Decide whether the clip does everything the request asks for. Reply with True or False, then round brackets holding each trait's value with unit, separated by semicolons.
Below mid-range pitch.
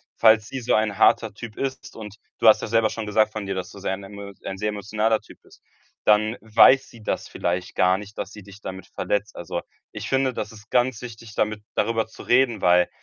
True (105 Hz)